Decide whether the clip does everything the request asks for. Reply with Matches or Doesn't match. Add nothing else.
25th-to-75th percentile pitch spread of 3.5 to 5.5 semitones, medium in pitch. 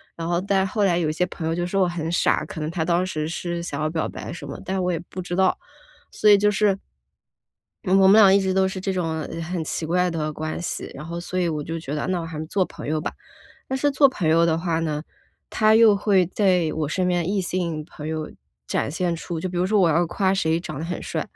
Doesn't match